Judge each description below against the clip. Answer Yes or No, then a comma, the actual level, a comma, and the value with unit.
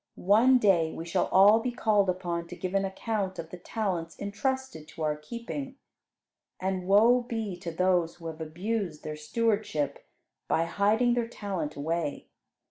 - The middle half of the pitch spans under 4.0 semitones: No, average, 5.1 semitones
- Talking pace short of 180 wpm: Yes, average, 160 wpm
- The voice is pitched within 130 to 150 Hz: No, high, 190 Hz